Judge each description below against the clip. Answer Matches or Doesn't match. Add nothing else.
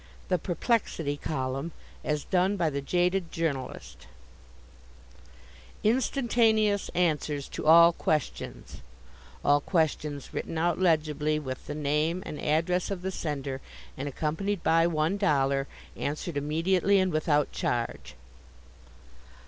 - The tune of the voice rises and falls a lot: Doesn't match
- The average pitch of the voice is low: Doesn't match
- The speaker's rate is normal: Doesn't match